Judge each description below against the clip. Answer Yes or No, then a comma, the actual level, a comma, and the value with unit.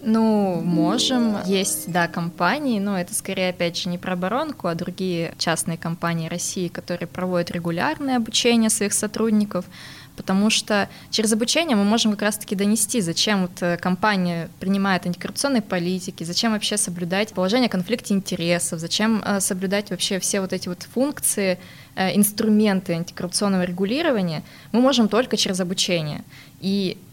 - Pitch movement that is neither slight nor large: Yes, average, 3.4 semitones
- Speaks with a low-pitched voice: No, high, 195 Hz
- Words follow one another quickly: No, average, 135 wpm